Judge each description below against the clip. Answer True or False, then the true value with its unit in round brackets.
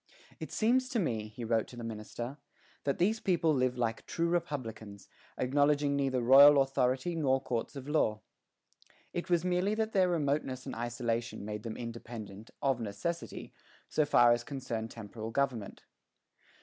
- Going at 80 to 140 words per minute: False (155 wpm)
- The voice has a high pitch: False (130 Hz)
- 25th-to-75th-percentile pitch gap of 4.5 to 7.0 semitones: True (5.0 semitones)